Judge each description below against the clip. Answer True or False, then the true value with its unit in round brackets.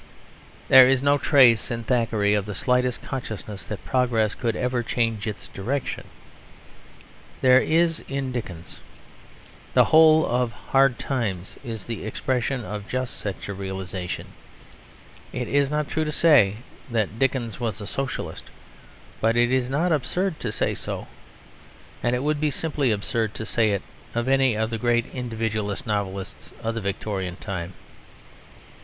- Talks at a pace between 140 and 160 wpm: True (150 wpm)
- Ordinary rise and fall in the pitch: True (4.1 semitones)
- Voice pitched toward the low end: True (120 Hz)